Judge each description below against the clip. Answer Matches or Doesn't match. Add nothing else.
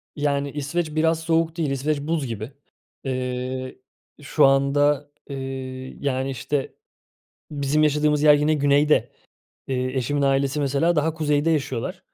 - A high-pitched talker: Doesn't match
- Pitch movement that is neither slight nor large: Doesn't match